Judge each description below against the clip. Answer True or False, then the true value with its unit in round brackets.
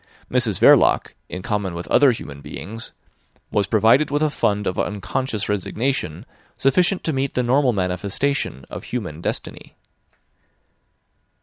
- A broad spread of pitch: True (6.0 semitones)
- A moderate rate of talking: False (130 wpm)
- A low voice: True (110 Hz)